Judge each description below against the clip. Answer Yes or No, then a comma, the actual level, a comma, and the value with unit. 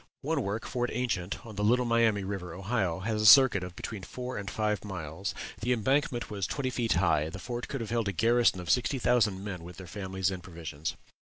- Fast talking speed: Yes, fast, 220 wpm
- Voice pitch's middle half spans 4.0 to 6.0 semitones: Yes, average, 4.4 semitones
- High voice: No, low, 105 Hz